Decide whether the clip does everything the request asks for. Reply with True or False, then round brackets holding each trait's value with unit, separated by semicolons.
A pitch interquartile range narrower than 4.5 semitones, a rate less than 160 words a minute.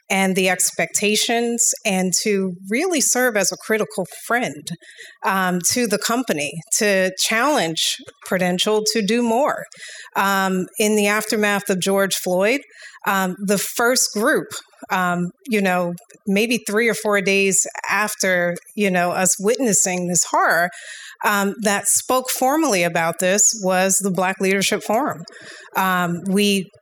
True (3.1 semitones; 135 wpm)